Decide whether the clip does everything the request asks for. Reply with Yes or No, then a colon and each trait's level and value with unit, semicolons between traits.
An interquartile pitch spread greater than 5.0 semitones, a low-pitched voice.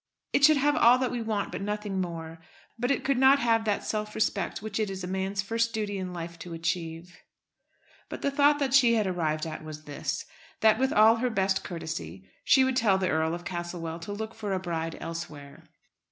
No: wide, 5.4 semitones; high, 195 Hz